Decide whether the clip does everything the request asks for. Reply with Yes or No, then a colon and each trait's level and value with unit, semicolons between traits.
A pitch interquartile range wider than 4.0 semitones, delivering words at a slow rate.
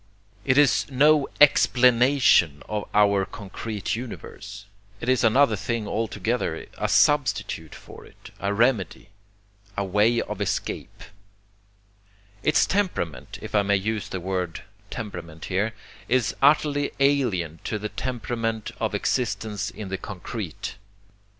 Yes: average, 4.6 semitones; slow, 125 wpm